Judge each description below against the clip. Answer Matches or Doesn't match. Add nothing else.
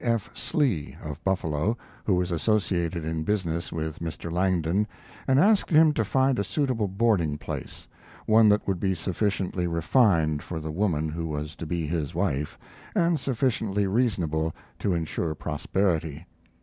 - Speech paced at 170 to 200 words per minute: Doesn't match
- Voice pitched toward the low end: Matches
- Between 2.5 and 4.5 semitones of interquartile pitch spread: Doesn't match